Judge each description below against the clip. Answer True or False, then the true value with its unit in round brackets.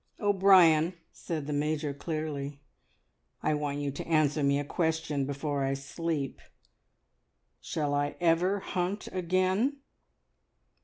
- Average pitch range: True (3.6 semitones)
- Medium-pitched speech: True (155 Hz)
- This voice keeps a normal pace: False (115 wpm)